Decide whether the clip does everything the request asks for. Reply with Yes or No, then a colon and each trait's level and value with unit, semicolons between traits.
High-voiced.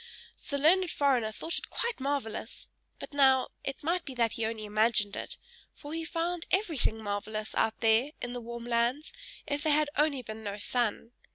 Yes: very high, 250 Hz